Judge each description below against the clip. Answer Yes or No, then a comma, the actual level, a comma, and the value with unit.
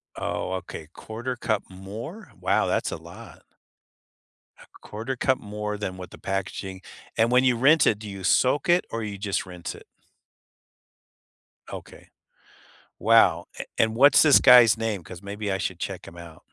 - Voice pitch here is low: Yes, low, 105 Hz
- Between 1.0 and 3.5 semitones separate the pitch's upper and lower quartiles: No, average, 4.1 semitones